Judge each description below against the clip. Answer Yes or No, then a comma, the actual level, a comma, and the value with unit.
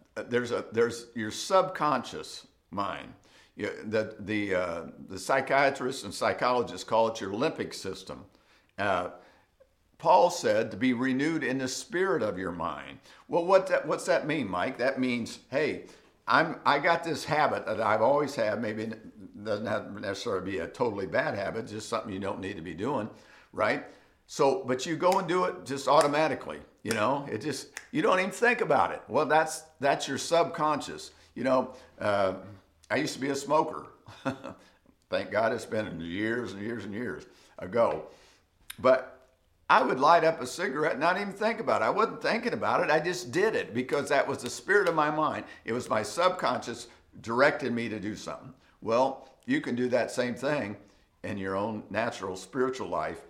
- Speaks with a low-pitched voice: Yes, low, 125 Hz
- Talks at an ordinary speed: Yes, average, 185 wpm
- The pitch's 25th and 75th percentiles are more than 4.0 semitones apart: Yes, wide, 5.6 semitones